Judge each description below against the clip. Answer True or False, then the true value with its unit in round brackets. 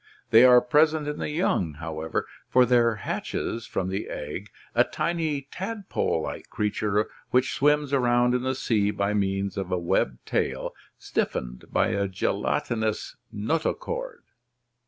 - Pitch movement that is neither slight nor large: False (7.1 semitones)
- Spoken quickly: False (140 wpm)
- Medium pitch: False (115 Hz)